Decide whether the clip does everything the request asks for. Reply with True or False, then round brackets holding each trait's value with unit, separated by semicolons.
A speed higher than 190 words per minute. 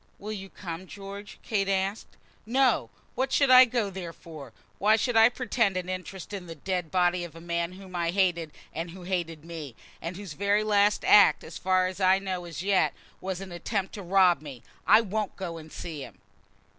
True (200 wpm)